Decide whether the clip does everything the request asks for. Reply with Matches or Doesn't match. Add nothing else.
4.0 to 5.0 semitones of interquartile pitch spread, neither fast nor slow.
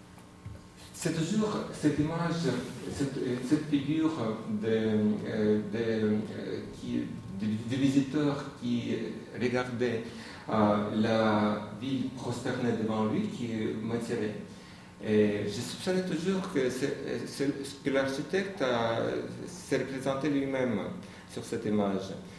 Doesn't match